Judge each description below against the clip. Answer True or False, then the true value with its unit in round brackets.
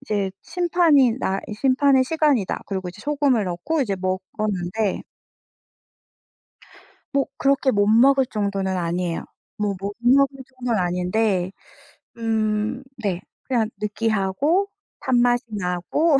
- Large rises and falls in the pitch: True (5.9 semitones)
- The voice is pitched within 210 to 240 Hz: True (220 Hz)